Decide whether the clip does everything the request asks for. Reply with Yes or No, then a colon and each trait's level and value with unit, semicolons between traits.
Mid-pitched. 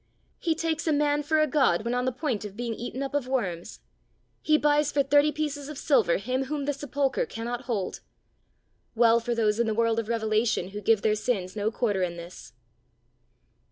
No: high, 245 Hz